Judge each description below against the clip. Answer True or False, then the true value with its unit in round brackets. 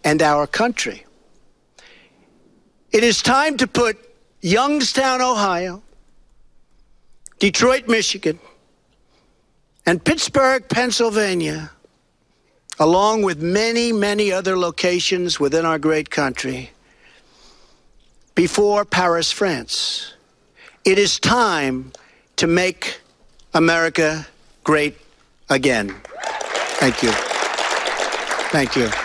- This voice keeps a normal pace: False (85 wpm)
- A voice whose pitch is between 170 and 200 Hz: True (185 Hz)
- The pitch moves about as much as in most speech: False (6.2 semitones)